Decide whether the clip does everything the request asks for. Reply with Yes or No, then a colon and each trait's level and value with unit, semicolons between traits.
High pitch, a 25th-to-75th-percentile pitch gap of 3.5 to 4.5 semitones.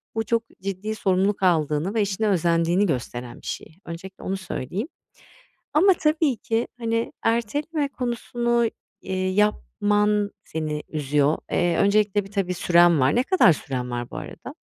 No: high, 195 Hz; average, 5.3 semitones